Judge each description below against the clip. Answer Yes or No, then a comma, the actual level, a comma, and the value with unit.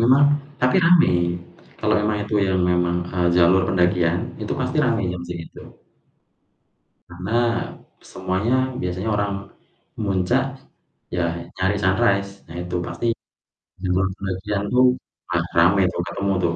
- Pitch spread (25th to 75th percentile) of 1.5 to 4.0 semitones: No, average, 4.4 semitones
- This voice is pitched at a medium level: No, low, 100 Hz